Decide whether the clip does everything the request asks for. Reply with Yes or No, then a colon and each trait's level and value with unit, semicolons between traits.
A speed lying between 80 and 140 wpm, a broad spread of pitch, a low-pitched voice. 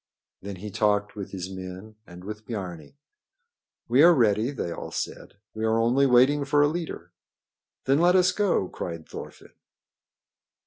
No: average, 160 wpm; wide, 6.6 semitones; low, 110 Hz